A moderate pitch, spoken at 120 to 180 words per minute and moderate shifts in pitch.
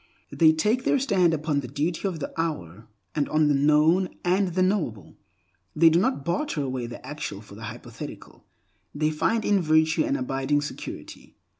Yes: medium, 160 Hz; average, 175 wpm; average, 4.4 semitones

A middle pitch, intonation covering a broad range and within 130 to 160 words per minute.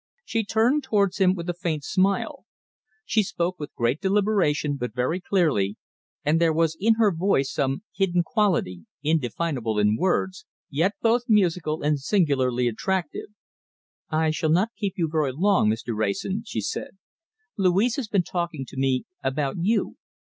Yes: medium, 170 Hz; wide, 6.1 semitones; average, 155 wpm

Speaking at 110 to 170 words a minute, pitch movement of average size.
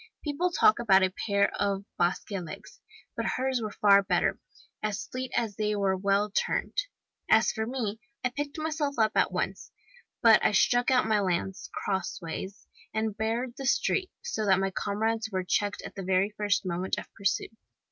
No: average, 180 wpm; average, 3.7 semitones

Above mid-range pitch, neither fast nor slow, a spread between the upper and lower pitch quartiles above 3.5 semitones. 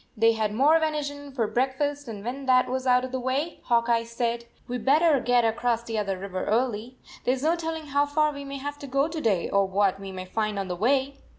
No: very high, 250 Hz; fast, 260 wpm; average, 4.3 semitones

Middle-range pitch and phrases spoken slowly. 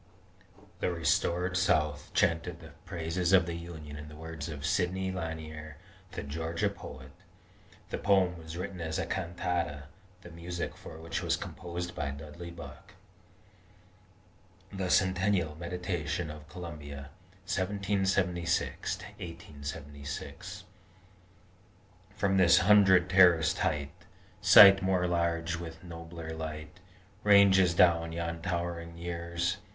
No: very low, 85 Hz; slow, 115 wpm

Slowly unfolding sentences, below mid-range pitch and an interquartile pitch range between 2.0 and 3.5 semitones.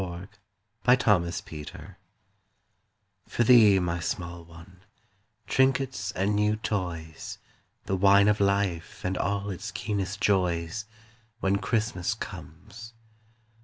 Yes: slow, 105 wpm; very low, 95 Hz; average, 3.2 semitones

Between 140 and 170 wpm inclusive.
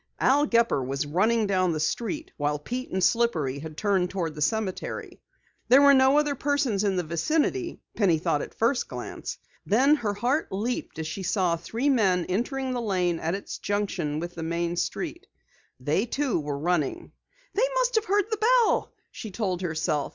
No: average, 180 wpm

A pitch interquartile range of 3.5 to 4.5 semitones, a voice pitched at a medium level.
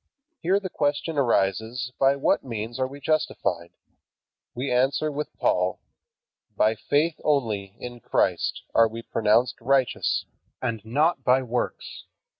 No: average, 4.1 semitones; low, 125 Hz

